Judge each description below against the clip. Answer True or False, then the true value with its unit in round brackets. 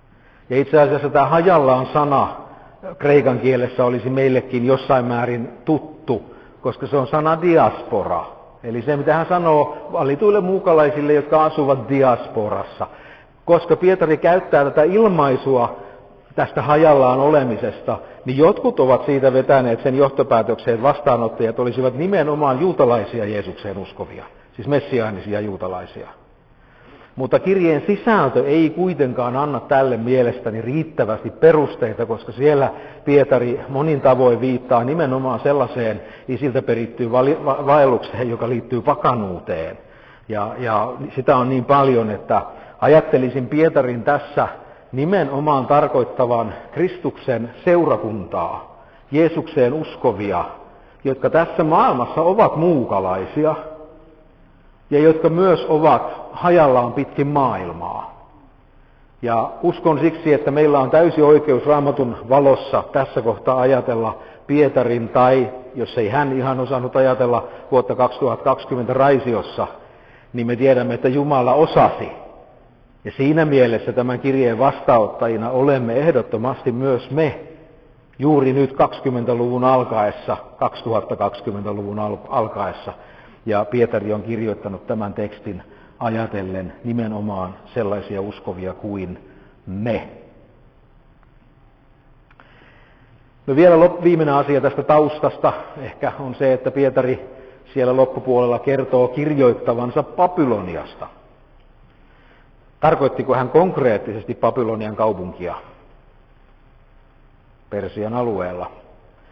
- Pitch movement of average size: True (3.8 semitones)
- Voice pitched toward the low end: True (130 Hz)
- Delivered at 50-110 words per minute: True (105 wpm)